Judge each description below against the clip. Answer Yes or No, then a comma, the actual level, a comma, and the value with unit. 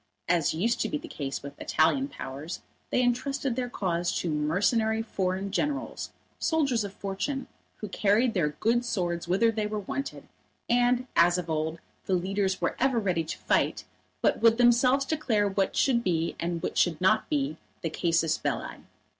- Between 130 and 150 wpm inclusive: No, average, 170 wpm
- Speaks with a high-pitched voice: Yes, high, 200 Hz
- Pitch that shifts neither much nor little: No, wide, 6.0 semitones